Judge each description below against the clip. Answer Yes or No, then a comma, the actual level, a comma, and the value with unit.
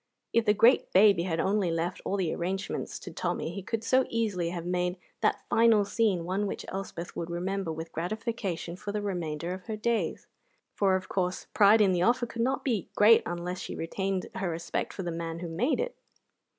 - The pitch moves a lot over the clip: No, average, 3.7 semitones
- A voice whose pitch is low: No, high, 190 Hz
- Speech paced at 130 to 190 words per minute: No, fast, 205 wpm